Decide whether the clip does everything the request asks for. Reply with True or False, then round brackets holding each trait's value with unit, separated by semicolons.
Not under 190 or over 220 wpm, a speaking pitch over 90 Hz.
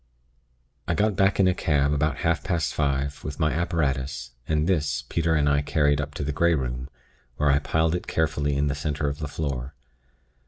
False (200 wpm; 75 Hz)